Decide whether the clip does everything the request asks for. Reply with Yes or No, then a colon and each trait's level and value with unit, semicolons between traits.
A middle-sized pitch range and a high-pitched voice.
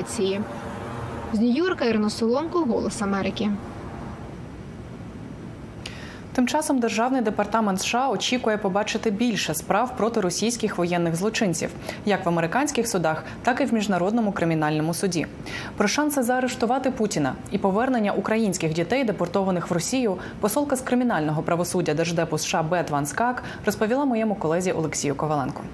No: wide, 5.7 semitones; high, 205 Hz